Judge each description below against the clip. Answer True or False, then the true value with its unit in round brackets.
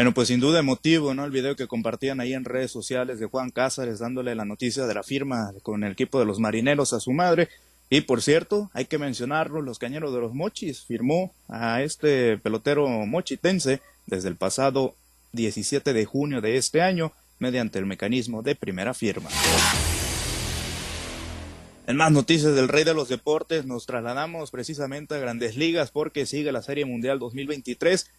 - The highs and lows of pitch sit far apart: False (4.1 semitones)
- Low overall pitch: True (130 Hz)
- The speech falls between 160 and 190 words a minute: True (175 wpm)